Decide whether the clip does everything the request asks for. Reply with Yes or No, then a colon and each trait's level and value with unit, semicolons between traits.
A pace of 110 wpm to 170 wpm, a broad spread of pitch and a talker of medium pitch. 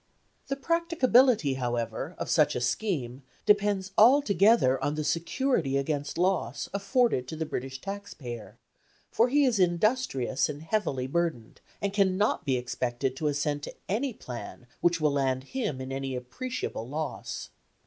Yes: average, 150 wpm; wide, 7.9 semitones; medium, 160 Hz